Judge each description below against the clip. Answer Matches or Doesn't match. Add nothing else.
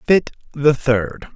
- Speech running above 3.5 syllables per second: Doesn't match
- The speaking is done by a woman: Doesn't match